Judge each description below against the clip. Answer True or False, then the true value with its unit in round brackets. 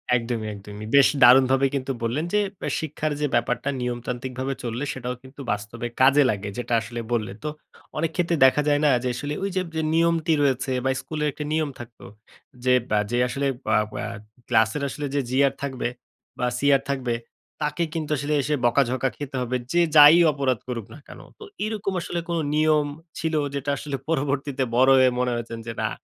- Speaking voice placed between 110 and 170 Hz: True (135 Hz)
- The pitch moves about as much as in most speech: True (3.5 semitones)